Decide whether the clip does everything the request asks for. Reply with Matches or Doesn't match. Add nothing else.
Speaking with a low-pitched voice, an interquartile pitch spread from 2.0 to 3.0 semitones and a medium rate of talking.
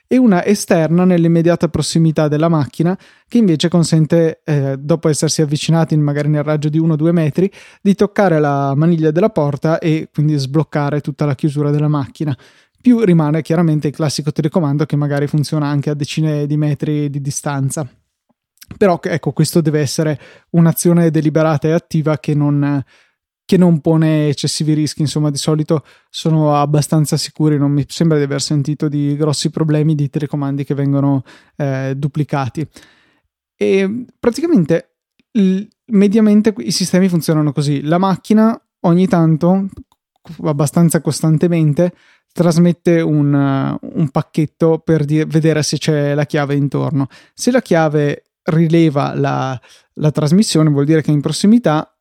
Doesn't match